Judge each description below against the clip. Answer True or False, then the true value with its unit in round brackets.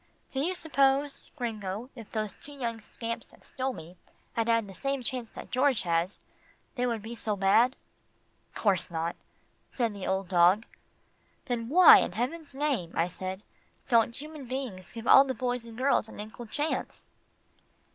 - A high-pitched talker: True (235 Hz)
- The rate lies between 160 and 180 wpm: True (165 wpm)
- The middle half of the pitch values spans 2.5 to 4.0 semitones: False (4.7 semitones)